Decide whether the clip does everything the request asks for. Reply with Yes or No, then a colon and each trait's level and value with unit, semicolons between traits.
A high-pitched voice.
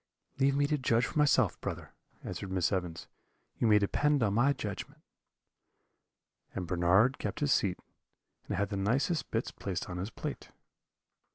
No: low, 110 Hz